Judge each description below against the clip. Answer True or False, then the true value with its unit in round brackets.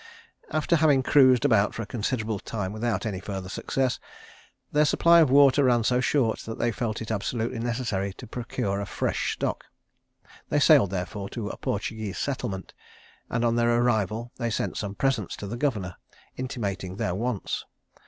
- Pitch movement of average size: True (4.0 semitones)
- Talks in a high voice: False (115 Hz)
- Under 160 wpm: False (170 wpm)